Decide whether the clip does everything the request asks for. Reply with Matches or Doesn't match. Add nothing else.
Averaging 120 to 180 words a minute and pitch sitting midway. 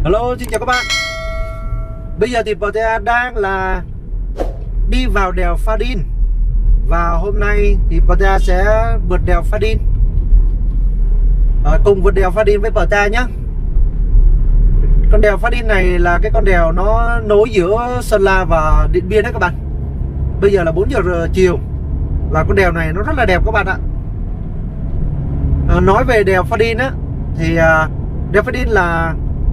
Matches